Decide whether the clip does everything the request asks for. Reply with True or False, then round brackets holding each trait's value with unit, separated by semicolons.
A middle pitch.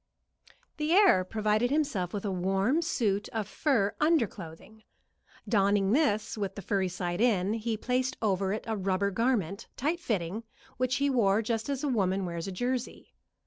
False (215 Hz)